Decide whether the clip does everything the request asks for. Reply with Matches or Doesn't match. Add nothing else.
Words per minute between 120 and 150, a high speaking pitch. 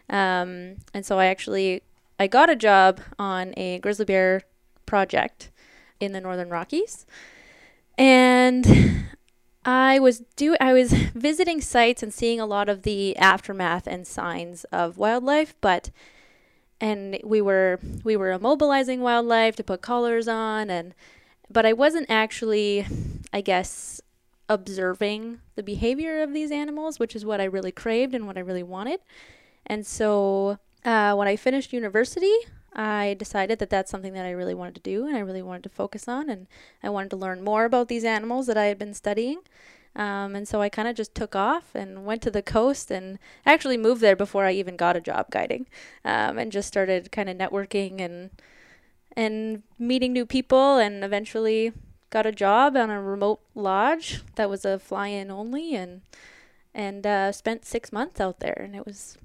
Doesn't match